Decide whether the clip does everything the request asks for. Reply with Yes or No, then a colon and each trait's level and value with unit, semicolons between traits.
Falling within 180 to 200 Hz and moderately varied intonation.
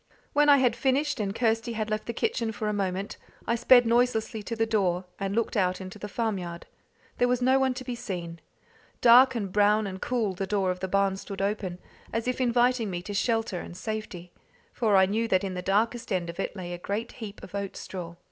No: high, 210 Hz; average, 3.6 semitones